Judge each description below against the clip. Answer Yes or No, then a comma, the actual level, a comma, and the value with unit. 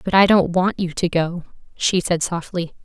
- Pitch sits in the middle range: Yes, medium, 180 Hz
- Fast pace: Yes, fast, 210 wpm